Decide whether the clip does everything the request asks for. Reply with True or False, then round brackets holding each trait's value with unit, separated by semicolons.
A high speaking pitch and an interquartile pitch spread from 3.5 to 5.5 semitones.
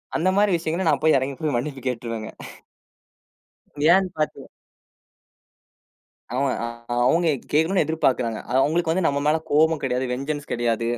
False (150 Hz; 4.0 semitones)